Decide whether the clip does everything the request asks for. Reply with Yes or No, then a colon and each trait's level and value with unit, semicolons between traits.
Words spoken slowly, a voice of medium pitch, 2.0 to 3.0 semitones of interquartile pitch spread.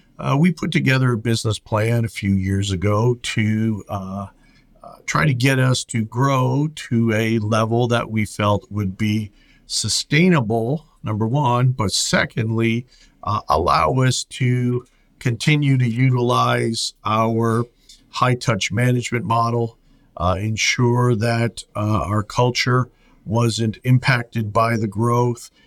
No: slow, 130 wpm; low, 115 Hz; narrow, 2.4 semitones